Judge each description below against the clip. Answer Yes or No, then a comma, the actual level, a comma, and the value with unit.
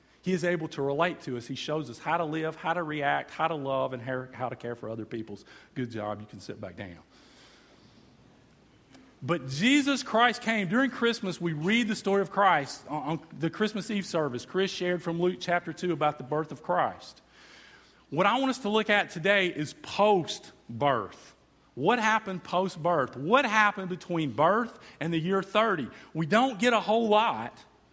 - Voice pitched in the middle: Yes, medium, 175 Hz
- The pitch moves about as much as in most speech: No, wide, 6.3 semitones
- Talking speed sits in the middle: Yes, average, 195 wpm